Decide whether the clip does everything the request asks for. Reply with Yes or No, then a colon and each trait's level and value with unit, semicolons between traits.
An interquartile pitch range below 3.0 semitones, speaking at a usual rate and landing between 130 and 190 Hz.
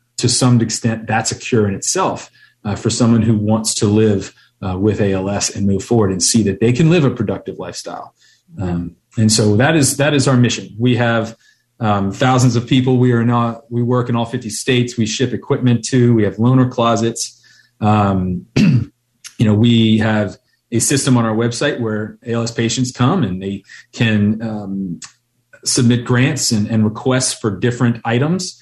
No: narrow, 2.6 semitones; average, 185 wpm; low, 115 Hz